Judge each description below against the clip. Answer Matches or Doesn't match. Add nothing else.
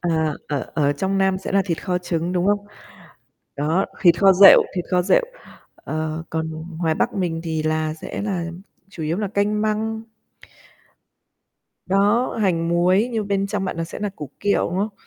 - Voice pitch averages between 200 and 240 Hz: Doesn't match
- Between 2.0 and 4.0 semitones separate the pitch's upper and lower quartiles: Matches